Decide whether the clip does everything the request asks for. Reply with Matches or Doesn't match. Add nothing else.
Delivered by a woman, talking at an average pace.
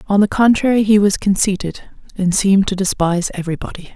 Matches